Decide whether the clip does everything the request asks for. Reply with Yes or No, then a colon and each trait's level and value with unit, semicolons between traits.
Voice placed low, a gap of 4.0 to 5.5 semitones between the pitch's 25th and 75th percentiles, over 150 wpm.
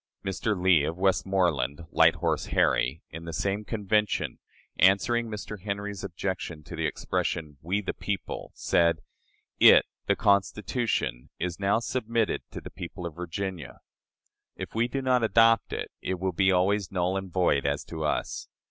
No: very low, 95 Hz; average, 3.5 semitones; average, 160 wpm